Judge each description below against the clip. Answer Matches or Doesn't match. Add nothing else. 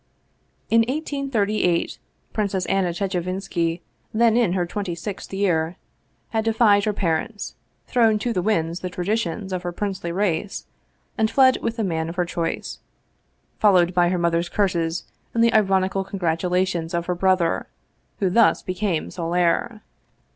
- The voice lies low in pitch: Doesn't match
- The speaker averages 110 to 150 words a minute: Matches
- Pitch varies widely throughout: Doesn't match